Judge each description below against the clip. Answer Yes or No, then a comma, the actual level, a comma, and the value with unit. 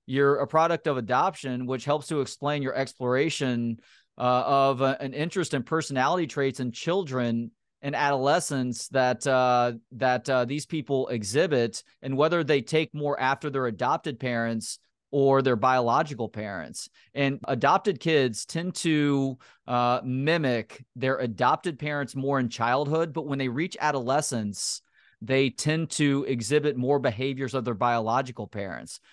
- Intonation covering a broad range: No, average, 2.8 semitones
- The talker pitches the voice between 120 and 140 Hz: Yes, low, 135 Hz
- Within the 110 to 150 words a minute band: Yes, average, 145 wpm